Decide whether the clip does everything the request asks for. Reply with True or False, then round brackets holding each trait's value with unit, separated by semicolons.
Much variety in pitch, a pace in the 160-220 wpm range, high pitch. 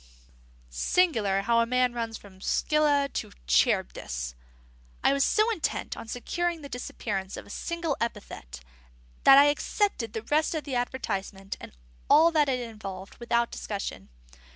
False (6.8 semitones; 150 wpm; 235 Hz)